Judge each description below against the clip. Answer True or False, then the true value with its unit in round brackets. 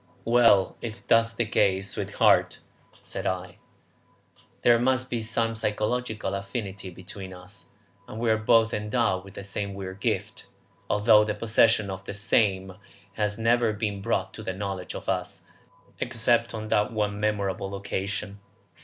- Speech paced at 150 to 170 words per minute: True (155 wpm)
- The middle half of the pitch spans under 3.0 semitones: True (2.5 semitones)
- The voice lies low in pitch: True (105 Hz)